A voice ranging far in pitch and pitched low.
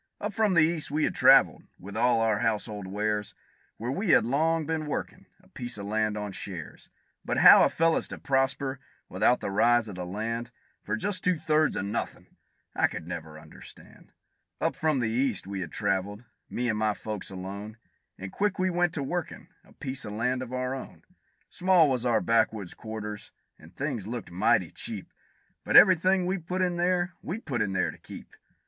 Yes: wide, 7.3 semitones; low, 120 Hz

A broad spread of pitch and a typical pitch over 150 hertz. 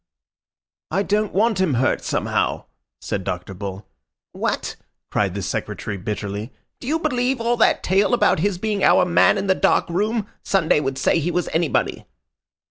Yes: wide, 8.3 semitones; medium, 185 Hz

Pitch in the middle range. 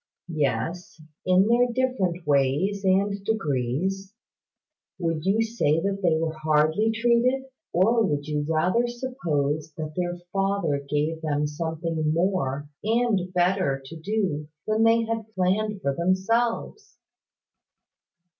Yes: medium, 180 Hz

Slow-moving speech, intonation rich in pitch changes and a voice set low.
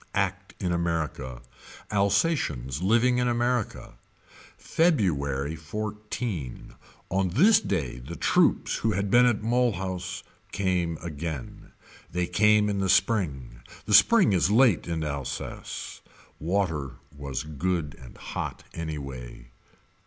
Yes: slow, 115 wpm; wide, 6.5 semitones; very low, 90 Hz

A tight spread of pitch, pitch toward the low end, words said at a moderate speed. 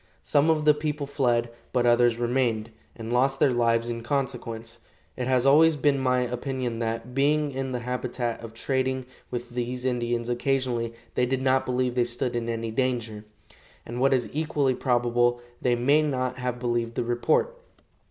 Yes: narrow, 1.9 semitones; low, 125 Hz; average, 170 wpm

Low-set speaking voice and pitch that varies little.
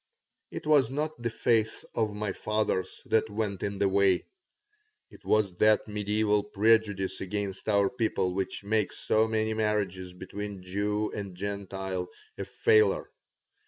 Yes: low, 105 Hz; narrow, 2.0 semitones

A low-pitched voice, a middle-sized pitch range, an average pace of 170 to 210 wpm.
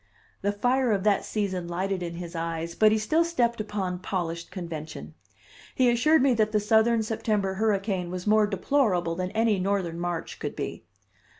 No: high, 200 Hz; average, 3.8 semitones; average, 175 wpm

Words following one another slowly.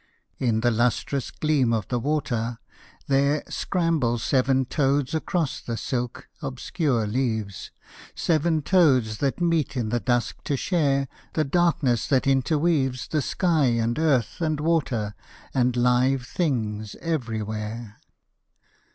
Yes: slow, 125 wpm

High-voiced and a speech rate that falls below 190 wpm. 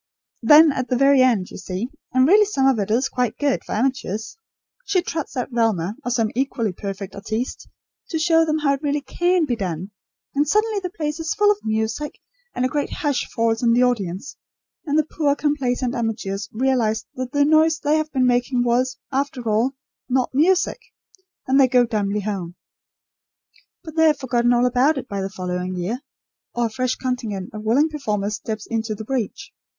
No: very high, 250 Hz; average, 195 wpm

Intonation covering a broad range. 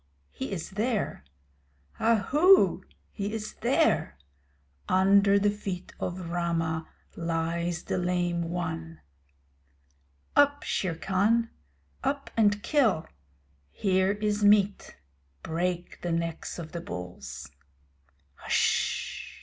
No: average, 3.7 semitones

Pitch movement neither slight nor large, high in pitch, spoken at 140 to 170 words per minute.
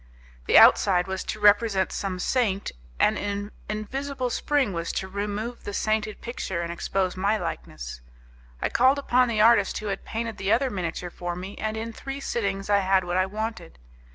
No: average, 3.3 semitones; high, 205 Hz; average, 180 wpm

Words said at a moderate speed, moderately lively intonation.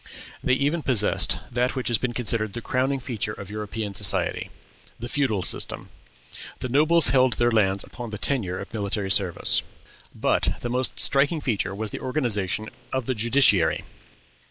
Yes: average, 160 wpm; average, 3.9 semitones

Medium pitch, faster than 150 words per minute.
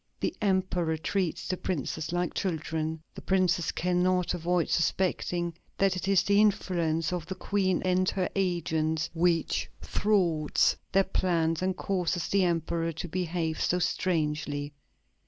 No: medium, 175 Hz; slow, 135 wpm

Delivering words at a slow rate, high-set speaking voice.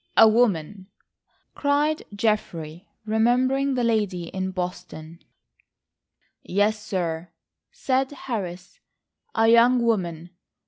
Yes: slow, 90 wpm; high, 215 Hz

